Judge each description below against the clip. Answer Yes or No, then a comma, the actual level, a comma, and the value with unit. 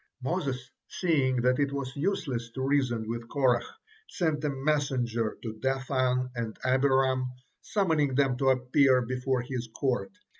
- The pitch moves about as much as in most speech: No, narrow, 2.0 semitones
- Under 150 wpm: Yes, average, 140 wpm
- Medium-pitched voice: No, low, 130 Hz